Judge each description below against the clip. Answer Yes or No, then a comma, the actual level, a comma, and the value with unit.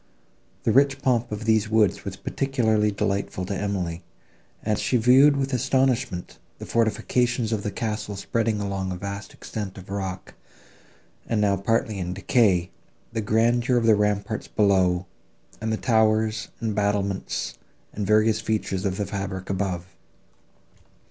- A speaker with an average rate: Yes, average, 145 wpm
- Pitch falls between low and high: No, low, 105 Hz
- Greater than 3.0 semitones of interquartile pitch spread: No, narrow, 2.6 semitones